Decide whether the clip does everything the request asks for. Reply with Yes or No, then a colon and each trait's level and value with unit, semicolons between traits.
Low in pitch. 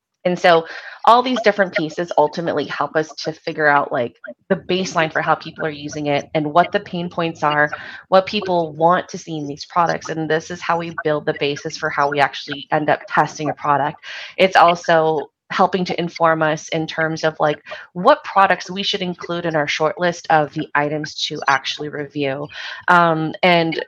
No: medium, 160 Hz